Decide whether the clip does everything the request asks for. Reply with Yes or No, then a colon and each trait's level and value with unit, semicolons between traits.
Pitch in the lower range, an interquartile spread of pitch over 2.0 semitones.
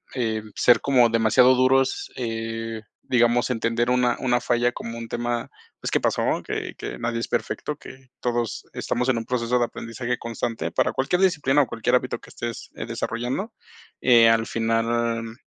No: low, 120 Hz; narrow, 1.6 semitones